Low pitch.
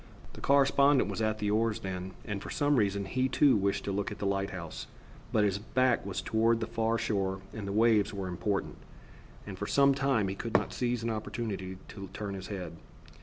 Yes: low, 105 Hz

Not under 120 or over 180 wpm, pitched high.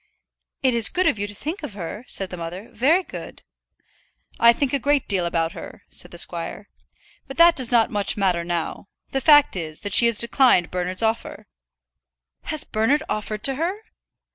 No: average, 190 wpm; high, 225 Hz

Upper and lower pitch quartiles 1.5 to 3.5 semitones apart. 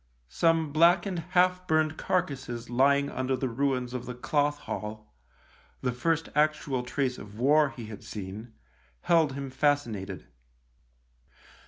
No: average, 4.3 semitones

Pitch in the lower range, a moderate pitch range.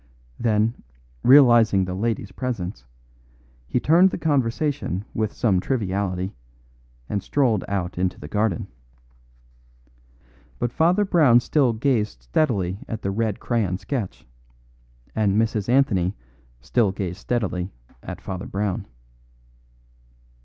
Yes: low, 110 Hz; average, 4.7 semitones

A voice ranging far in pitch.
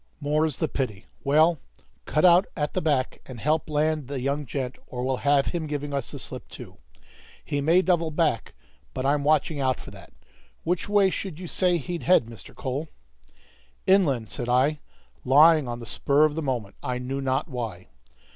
No: average, 3.6 semitones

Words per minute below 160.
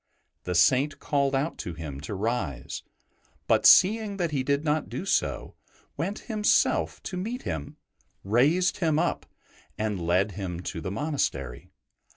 Yes: average, 145 wpm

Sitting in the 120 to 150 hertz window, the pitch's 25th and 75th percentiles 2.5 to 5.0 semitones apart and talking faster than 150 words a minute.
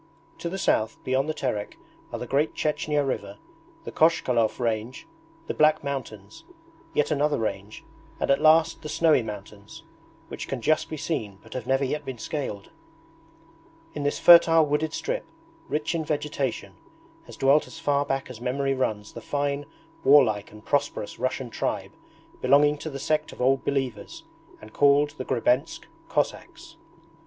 Yes: medium, 140 Hz; average, 4.0 semitones; average, 160 wpm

